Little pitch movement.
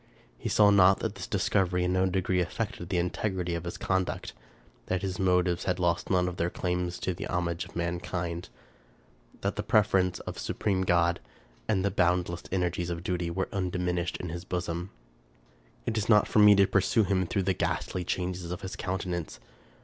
Yes: narrow, 1.5 semitones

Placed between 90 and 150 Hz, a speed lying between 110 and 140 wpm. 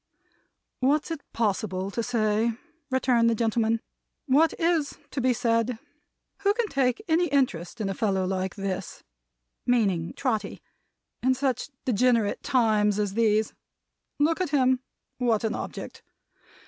No: high, 235 Hz; slow, 135 wpm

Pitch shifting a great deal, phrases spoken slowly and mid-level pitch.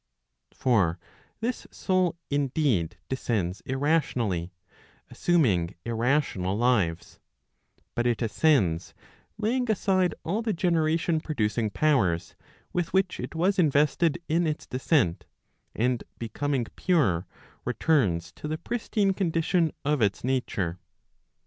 Yes: wide, 7.7 semitones; slow, 105 wpm; medium, 145 Hz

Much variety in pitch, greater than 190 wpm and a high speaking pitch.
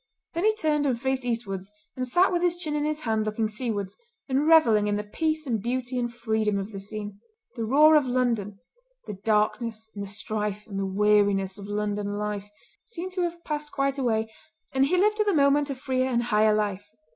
Yes: wide, 5.9 semitones; average, 200 wpm; high, 235 Hz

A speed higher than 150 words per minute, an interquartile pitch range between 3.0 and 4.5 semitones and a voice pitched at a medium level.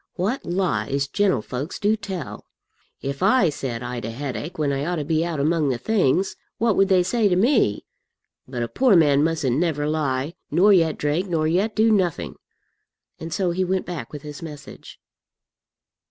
No: average, 180 wpm; average, 5.2 semitones; medium, 165 Hz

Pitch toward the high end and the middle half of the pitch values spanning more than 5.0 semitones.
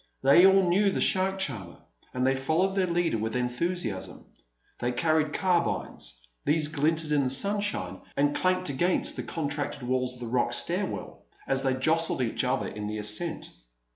No: medium, 145 Hz; wide, 5.6 semitones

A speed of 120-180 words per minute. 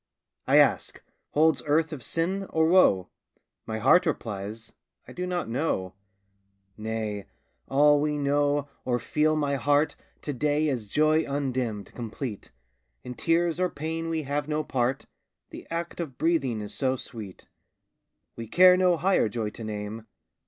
Yes: average, 150 wpm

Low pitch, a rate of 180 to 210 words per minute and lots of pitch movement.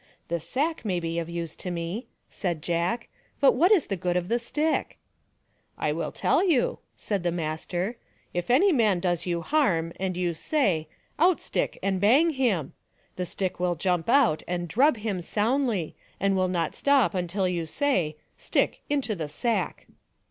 No: medium, 185 Hz; average, 200 wpm; wide, 6.3 semitones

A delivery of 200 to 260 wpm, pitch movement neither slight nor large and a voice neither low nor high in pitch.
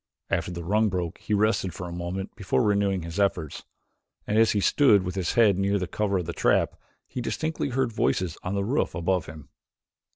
No: fast, 205 wpm; average, 3.1 semitones; very low, 95 Hz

